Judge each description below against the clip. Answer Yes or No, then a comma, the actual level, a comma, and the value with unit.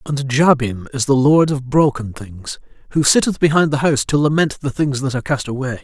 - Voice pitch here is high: No, low, 135 Hz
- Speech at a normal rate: No, fast, 215 wpm